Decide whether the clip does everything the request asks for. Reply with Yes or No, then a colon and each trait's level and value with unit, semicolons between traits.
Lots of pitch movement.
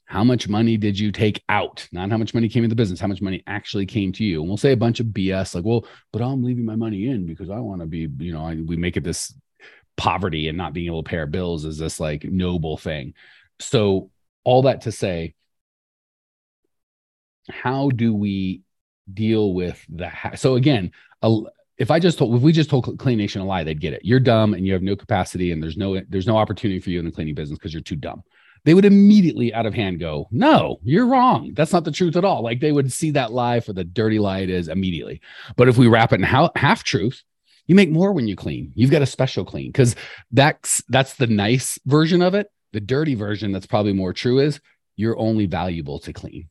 Yes: wide, 5.9 semitones